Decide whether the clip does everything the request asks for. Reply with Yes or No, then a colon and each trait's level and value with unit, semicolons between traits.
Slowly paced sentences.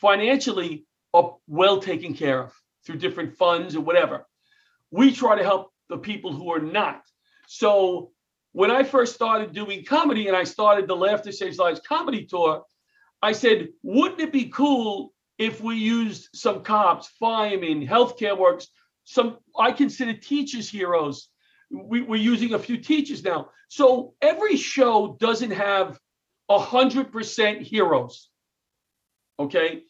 No: average, 145 wpm